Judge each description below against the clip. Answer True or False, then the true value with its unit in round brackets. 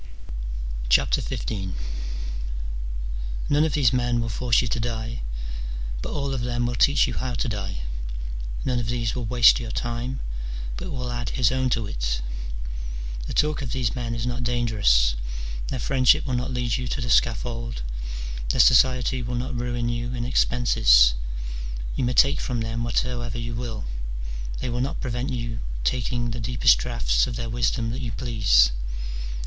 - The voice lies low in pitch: True (120 Hz)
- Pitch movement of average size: False (1.5 semitones)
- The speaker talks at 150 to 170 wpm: True (165 wpm)